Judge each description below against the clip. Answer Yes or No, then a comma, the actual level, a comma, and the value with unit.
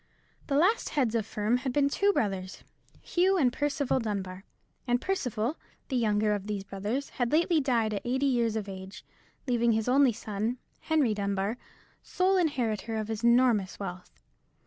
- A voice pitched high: Yes, high, 235 Hz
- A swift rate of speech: No, average, 170 wpm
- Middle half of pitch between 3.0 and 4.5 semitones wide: No, average, 5.0 semitones